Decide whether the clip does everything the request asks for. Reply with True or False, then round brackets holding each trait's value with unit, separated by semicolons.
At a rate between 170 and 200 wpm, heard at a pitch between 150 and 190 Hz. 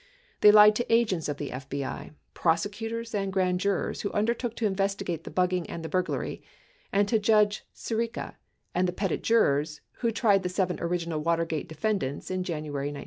True (180 wpm; 185 Hz)